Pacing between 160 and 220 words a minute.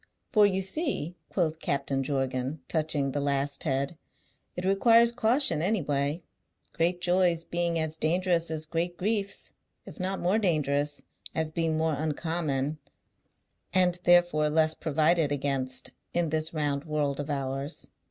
No: average, 140 wpm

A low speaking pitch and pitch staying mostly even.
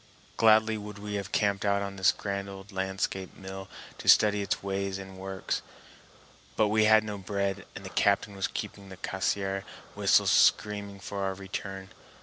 Yes: low, 100 Hz; narrow, 1.1 semitones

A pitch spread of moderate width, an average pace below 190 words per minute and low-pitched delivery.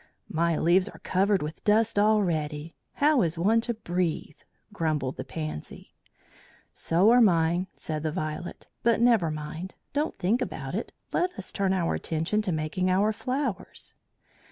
No: average, 5.0 semitones; average, 155 wpm; medium, 185 Hz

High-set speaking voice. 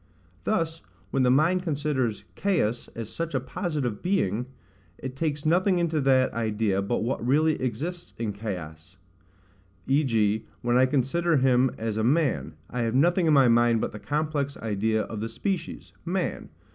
No: low, 130 Hz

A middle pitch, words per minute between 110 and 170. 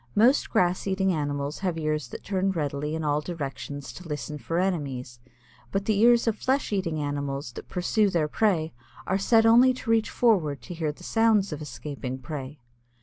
No: medium, 165 Hz; average, 185 wpm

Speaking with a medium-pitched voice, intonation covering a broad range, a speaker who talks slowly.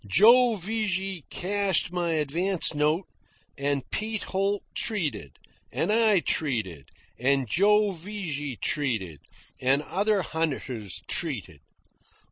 Yes: medium, 170 Hz; wide, 6.6 semitones; slow, 100 wpm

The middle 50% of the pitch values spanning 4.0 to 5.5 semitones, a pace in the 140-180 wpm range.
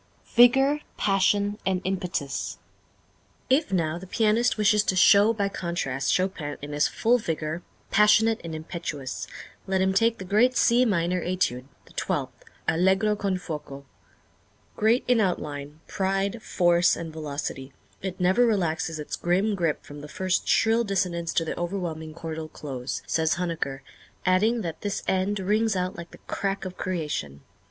Yes: average, 4.3 semitones; average, 150 wpm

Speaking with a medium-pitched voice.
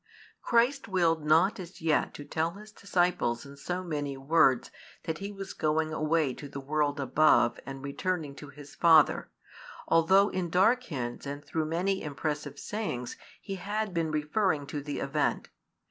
Yes: medium, 160 Hz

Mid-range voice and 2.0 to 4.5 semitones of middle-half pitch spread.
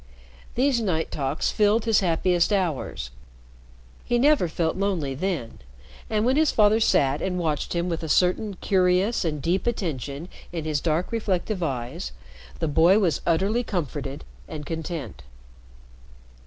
No: medium, 175 Hz; average, 5.2 semitones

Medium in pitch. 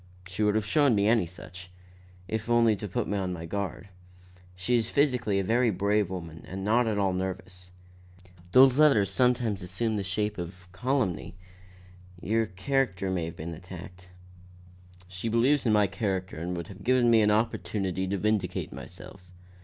No: low, 100 Hz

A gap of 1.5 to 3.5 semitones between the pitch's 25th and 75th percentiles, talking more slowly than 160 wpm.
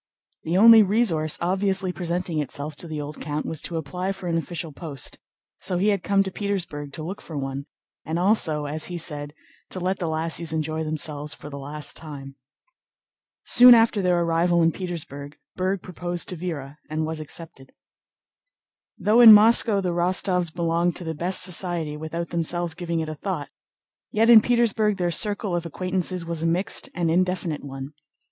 No: average, 3.1 semitones; average, 180 wpm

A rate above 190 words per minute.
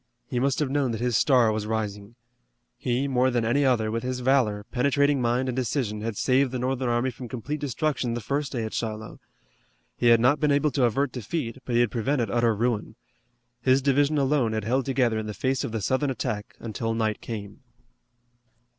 Yes: fast, 205 wpm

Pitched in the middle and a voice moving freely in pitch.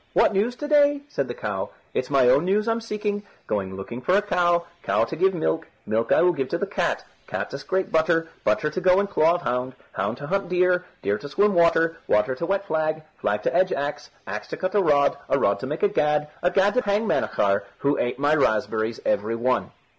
Yes: medium, 165 Hz; wide, 6.7 semitones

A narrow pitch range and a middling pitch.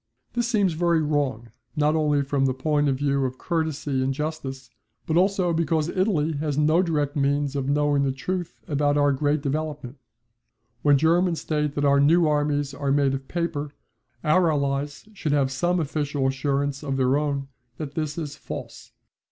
Yes: narrow, 2.2 semitones; medium, 145 Hz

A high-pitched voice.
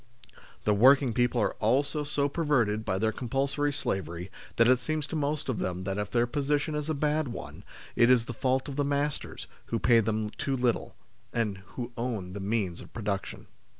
No: low, 125 Hz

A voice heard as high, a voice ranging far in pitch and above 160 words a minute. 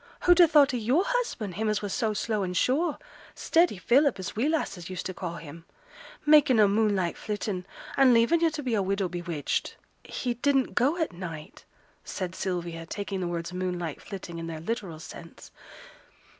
Yes: high, 205 Hz; wide, 6.8 semitones; average, 185 wpm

